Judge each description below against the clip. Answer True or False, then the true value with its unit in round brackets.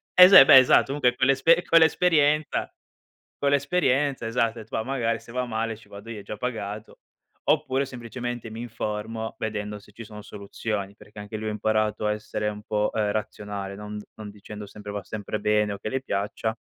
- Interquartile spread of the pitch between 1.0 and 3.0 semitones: False (3.4 semitones)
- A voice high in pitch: False (110 Hz)